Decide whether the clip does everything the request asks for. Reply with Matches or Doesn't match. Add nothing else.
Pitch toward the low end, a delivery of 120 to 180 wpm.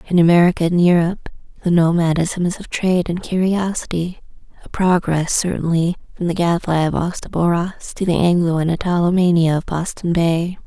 Doesn't match